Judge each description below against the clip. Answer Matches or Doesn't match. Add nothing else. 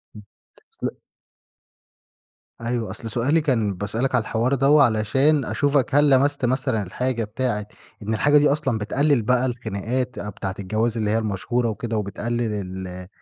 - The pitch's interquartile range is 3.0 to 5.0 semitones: Matches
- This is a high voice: Doesn't match